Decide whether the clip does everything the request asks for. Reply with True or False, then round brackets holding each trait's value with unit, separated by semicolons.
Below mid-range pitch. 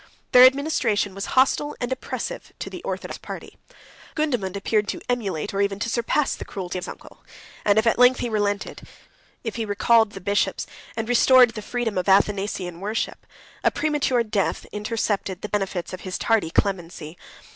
False (210 Hz)